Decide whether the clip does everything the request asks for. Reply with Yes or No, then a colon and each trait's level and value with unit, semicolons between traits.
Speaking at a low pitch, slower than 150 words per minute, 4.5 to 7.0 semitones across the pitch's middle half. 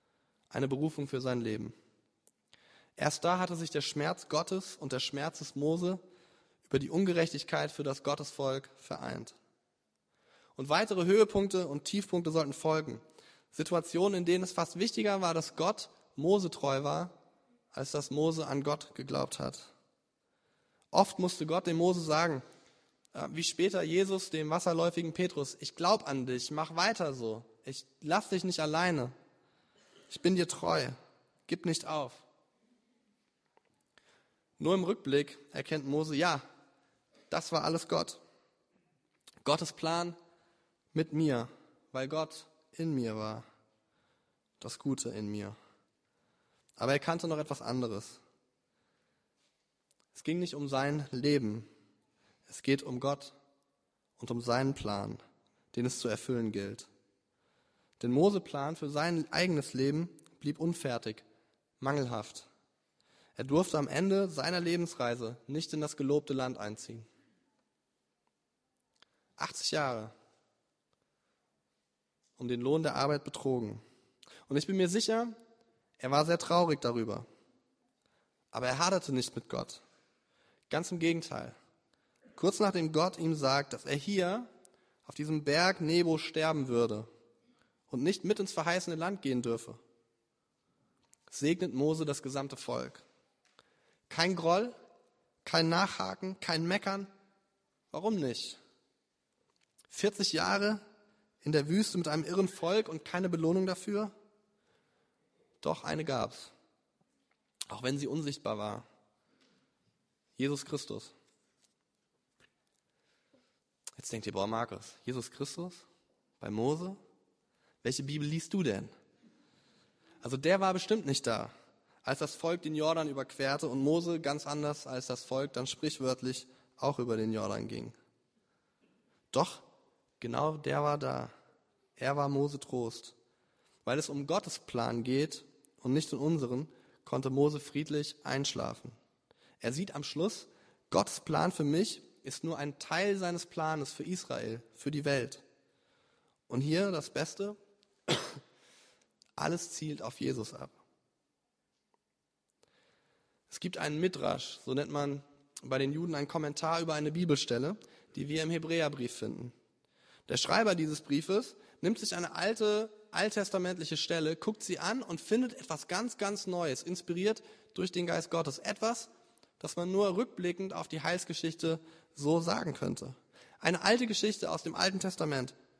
No: medium, 155 Hz; average, 135 wpm; average, 4.9 semitones